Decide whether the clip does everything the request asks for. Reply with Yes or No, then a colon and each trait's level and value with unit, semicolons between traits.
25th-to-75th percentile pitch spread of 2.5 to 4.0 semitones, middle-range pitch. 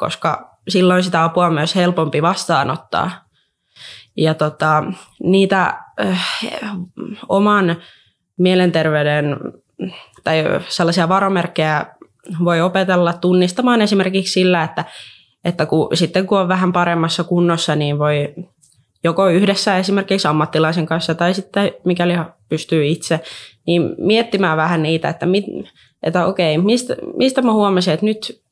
Yes: average, 3.1 semitones; medium, 175 Hz